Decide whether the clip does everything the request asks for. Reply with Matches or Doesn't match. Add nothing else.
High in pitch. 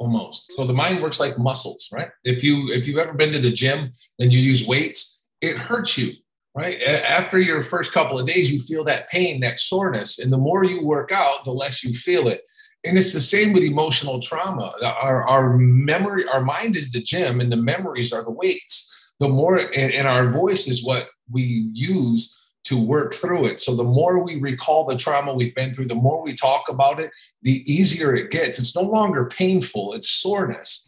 Doesn't match